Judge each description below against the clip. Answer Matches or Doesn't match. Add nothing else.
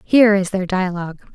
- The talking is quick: Doesn't match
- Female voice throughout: Matches